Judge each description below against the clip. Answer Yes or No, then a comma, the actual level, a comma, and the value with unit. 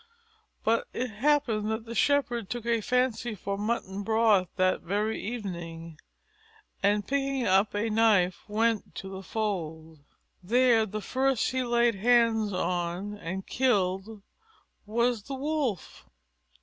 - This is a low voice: No, high, 220 Hz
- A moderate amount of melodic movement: Yes, average, 3.7 semitones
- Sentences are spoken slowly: Yes, slow, 130 wpm